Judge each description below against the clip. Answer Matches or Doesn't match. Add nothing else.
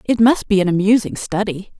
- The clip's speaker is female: Matches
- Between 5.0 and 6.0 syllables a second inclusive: Matches